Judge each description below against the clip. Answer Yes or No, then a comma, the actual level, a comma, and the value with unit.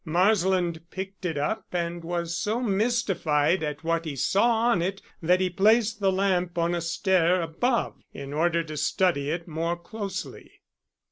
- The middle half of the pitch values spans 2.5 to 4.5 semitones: Yes, average, 3.0 semitones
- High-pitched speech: No, medium, 175 Hz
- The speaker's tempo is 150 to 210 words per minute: Yes, average, 160 wpm